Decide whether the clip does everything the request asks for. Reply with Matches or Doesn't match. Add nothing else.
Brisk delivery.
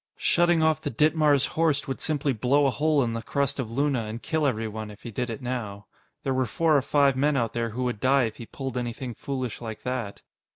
Matches